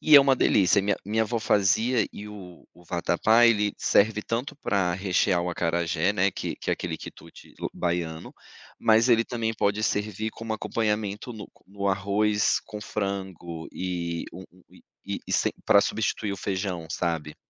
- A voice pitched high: No, low, 100 Hz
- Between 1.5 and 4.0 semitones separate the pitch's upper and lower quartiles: Yes, average, 3.4 semitones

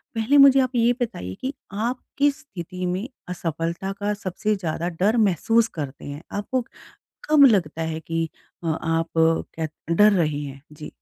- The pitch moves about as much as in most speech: No, wide, 6.0 semitones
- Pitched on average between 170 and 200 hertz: Yes, medium, 185 Hz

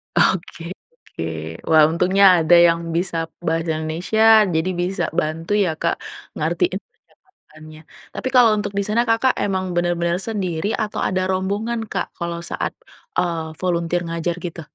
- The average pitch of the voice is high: No, medium, 175 Hz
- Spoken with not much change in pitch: No, average, 3.6 semitones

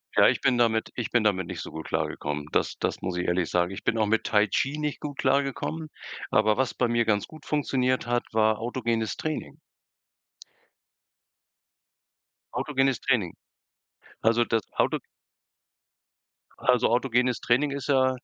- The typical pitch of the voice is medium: No, low, 120 Hz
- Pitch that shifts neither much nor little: Yes, average, 3.6 semitones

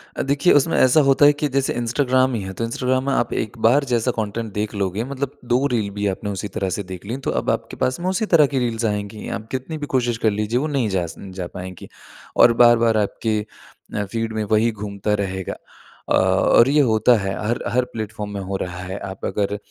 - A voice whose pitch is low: Yes, low, 115 Hz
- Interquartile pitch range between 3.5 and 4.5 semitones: Yes, average, 4.1 semitones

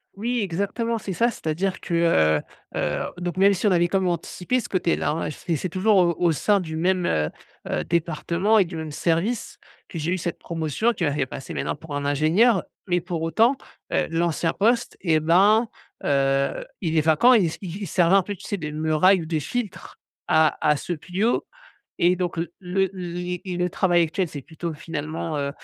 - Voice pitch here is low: No, medium, 175 Hz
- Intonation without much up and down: No, average, 3.5 semitones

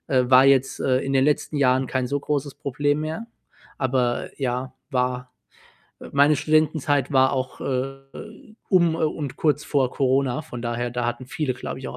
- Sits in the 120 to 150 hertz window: Yes, low, 135 Hz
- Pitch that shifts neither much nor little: No, narrow, 2.3 semitones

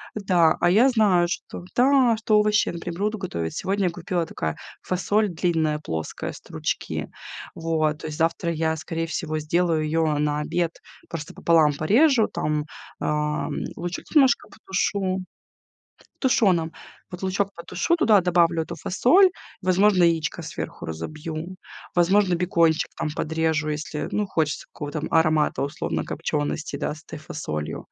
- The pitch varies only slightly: No, average, 3.7 semitones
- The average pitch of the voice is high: No, medium, 170 Hz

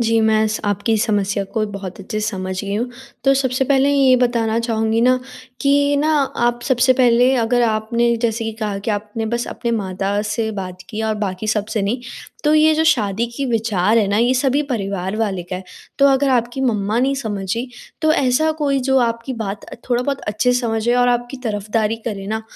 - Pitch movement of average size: Yes, average, 3.3 semitones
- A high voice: Yes, high, 230 Hz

